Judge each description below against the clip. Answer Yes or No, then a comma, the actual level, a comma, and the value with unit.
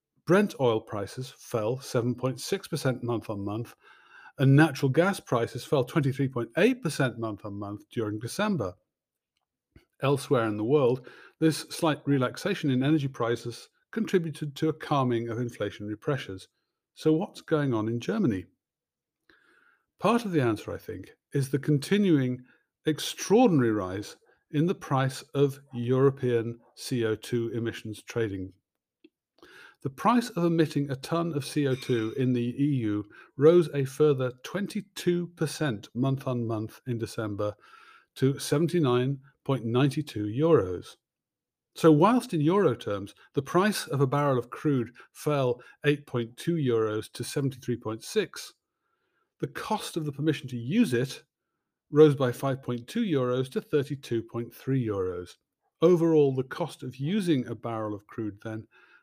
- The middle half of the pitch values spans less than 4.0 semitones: No, average, 4.9 semitones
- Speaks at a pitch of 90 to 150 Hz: Yes, low, 135 Hz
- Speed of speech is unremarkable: No, slow, 130 wpm